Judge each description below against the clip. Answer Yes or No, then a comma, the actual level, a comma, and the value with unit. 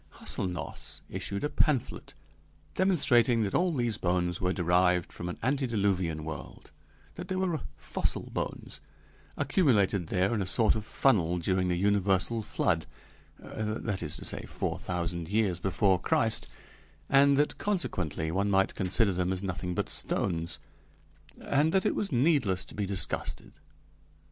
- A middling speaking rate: Yes, average, 145 wpm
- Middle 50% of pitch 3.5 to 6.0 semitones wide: Yes, average, 5.0 semitones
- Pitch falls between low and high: No, low, 100 Hz